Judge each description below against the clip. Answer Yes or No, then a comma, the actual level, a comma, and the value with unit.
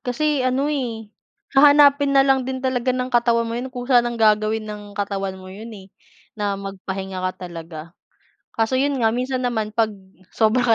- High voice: Yes, high, 230 Hz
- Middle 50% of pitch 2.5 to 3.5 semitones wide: No, average, 4.4 semitones